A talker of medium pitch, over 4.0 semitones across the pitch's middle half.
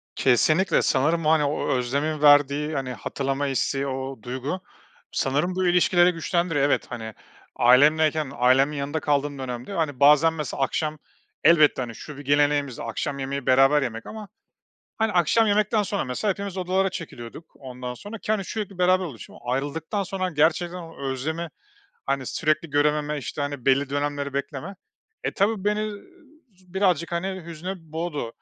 Yes: medium, 150 Hz; average, 4.4 semitones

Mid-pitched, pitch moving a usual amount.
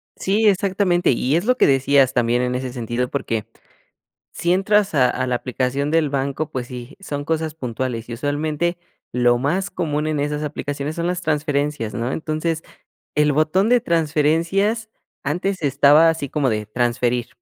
Yes: medium, 150 Hz; average, 4.5 semitones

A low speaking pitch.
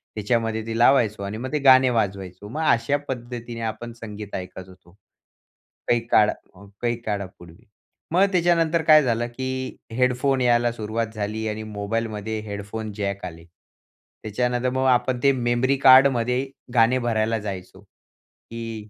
Yes: low, 115 Hz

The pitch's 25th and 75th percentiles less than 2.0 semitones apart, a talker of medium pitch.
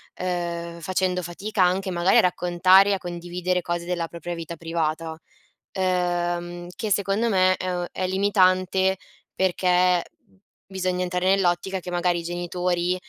Yes: narrow, 1.2 semitones; medium, 180 Hz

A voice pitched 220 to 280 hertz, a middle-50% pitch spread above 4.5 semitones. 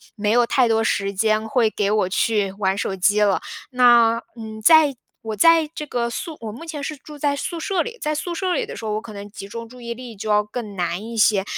Yes: high, 225 Hz; average, 5.2 semitones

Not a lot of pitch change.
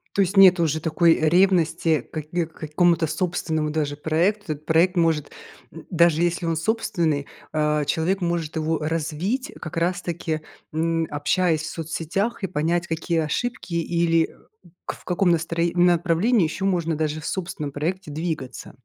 Yes: narrow, 2.2 semitones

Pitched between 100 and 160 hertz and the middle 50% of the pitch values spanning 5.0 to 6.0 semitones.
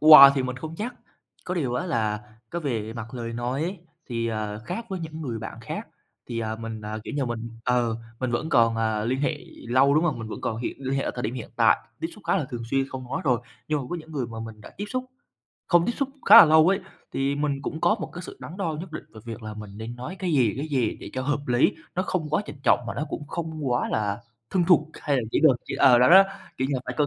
Yes: low, 135 Hz; average, 5.3 semitones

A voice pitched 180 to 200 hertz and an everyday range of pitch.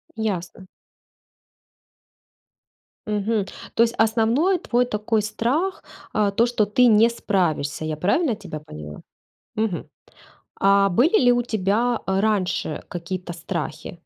No: high, 210 Hz; average, 4.3 semitones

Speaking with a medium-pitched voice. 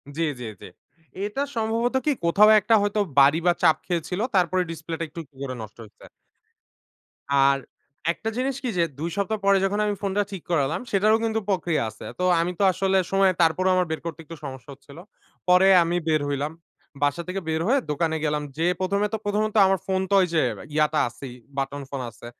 Yes: medium, 175 Hz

